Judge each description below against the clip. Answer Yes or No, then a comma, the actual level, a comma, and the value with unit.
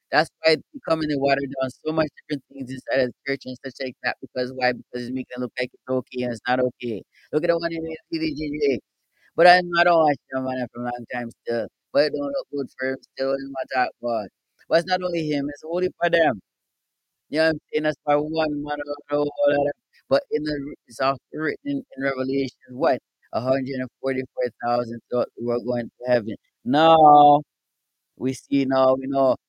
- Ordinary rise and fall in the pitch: Yes, average, 3.3 semitones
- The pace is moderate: No, fast, 220 wpm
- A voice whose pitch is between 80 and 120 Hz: No, low, 135 Hz